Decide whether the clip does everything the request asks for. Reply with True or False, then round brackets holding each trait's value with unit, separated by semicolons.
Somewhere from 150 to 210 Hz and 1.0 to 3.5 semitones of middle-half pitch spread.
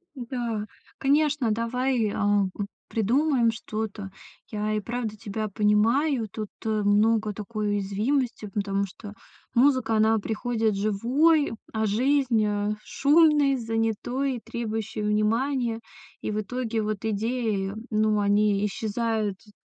False (220 Hz; 2.8 semitones)